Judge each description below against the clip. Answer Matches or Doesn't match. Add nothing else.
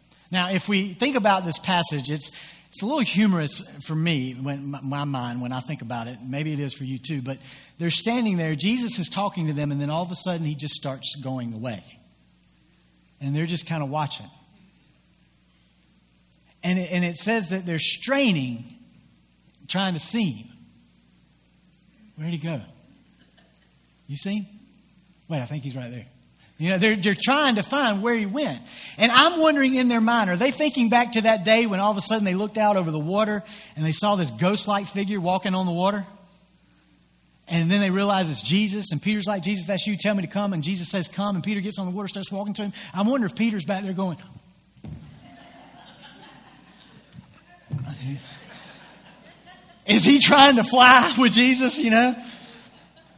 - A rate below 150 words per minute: Doesn't match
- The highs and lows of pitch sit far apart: Matches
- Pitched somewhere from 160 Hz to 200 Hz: Matches